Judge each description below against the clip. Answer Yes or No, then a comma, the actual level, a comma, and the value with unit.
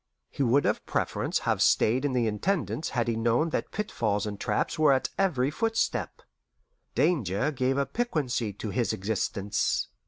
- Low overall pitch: Yes, low, 130 Hz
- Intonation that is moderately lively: No, wide, 5.7 semitones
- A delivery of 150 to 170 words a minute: Yes, average, 160 wpm